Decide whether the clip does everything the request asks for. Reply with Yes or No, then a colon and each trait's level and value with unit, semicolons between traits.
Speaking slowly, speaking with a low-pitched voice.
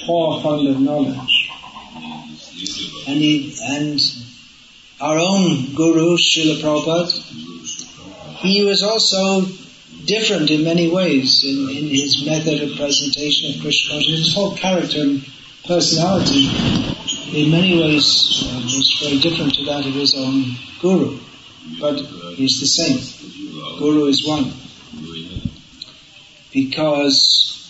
No: slow, 115 wpm; medium, 145 Hz